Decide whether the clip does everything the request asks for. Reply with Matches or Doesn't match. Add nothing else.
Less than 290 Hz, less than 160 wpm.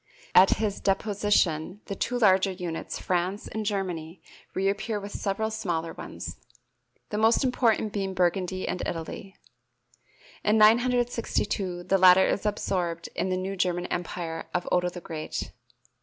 Matches